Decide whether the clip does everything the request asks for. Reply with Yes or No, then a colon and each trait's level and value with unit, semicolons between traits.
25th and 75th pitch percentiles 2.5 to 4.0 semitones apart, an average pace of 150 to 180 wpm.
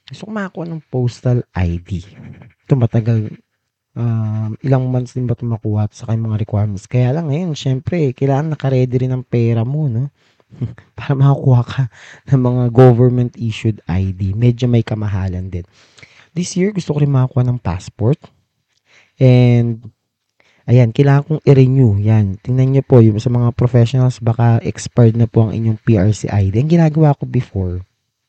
Yes: average, 3.4 semitones; fast, 155 wpm